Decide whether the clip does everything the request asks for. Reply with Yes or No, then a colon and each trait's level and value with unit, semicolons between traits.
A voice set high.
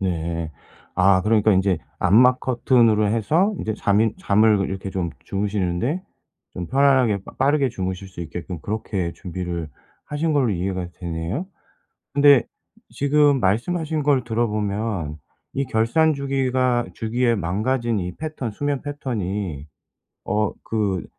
No: low, 110 Hz